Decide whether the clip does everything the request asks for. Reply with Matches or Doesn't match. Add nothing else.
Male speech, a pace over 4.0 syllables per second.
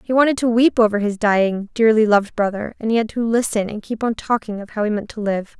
Doesn't match